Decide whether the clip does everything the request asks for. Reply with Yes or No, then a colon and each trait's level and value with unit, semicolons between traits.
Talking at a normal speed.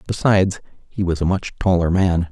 Yes: average, 180 wpm